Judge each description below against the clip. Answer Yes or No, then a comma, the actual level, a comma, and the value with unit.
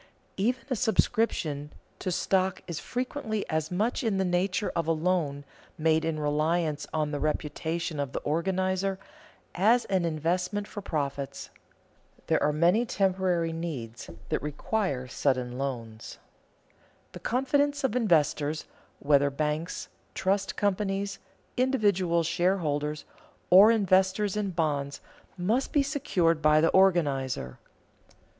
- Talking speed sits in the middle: No, slow, 125 wpm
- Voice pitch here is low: No, medium, 175 Hz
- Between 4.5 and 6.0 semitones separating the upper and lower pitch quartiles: Yes, average, 4.8 semitones